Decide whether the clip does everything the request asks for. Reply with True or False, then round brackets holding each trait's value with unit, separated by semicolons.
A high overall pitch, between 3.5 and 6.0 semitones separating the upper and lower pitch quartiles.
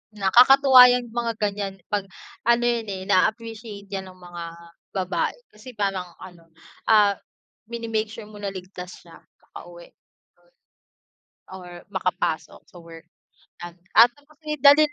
True (210 Hz; 4.1 semitones)